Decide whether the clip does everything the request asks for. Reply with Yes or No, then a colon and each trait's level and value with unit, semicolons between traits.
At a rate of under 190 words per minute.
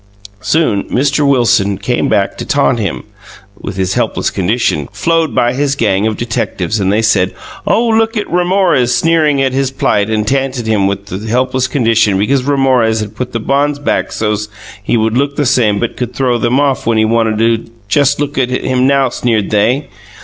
No: average, 195 wpm